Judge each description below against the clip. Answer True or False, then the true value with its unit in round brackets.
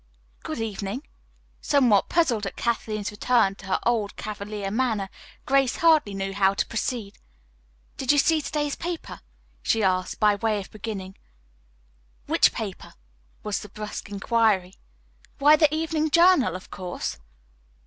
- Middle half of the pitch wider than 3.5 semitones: True (5.6 semitones)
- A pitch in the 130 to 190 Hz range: False (215 Hz)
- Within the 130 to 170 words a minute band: True (140 wpm)